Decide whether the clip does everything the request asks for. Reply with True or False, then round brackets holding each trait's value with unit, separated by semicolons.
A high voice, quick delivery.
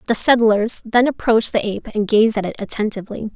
False (220 Hz; 195 wpm)